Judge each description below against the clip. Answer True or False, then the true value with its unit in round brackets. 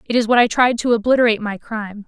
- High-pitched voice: True (225 Hz)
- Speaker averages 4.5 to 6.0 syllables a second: False (7.2 syllables/s)